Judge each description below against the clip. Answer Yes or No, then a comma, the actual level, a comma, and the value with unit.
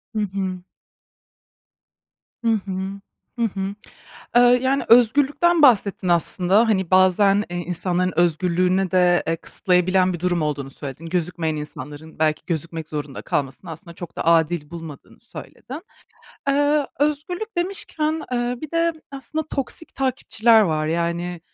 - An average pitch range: No, wide, 6.8 semitones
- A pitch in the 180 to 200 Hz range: Yes, medium, 185 Hz